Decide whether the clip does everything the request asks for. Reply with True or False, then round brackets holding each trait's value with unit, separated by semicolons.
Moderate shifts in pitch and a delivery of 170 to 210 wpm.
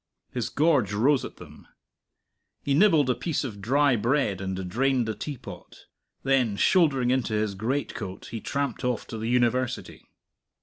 False (4.2 semitones; 155 wpm)